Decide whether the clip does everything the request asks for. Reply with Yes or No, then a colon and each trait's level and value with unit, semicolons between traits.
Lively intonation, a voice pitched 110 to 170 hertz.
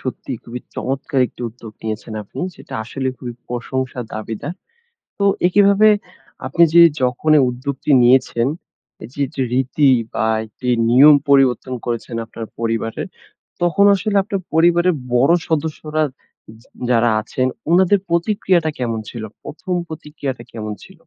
Yes: wide, 5.8 semitones; low, 135 Hz